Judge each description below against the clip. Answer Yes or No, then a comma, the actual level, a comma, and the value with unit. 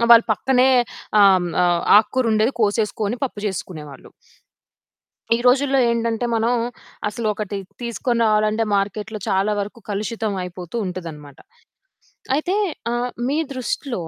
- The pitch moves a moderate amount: Yes, average, 3.2 semitones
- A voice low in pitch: No, high, 215 Hz